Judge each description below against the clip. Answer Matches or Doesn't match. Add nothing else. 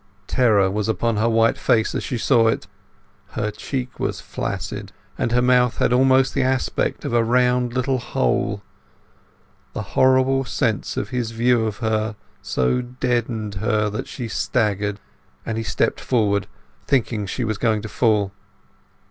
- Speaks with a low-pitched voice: Matches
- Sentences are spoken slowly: Doesn't match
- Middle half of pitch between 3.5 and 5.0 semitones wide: Doesn't match